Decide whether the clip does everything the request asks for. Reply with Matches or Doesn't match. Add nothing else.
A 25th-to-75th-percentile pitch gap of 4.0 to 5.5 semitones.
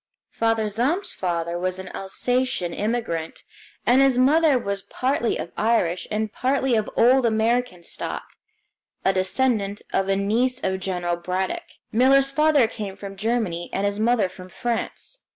Matches